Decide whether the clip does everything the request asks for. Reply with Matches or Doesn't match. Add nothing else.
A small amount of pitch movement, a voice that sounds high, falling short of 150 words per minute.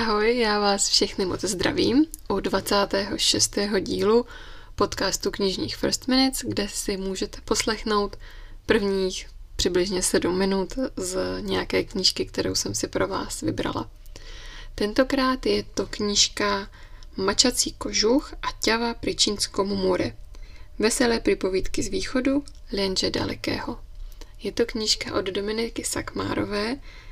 Doesn't match